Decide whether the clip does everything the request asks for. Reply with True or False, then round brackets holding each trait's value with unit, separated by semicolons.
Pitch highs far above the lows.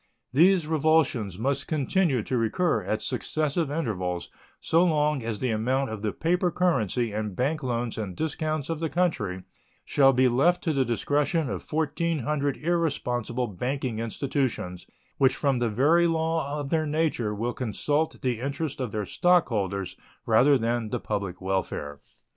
True (6.0 semitones)